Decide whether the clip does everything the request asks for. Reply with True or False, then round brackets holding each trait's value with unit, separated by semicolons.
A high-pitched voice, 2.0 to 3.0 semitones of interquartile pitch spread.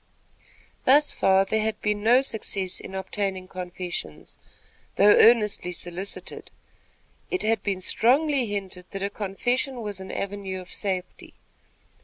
True (200 Hz; 2.7 semitones)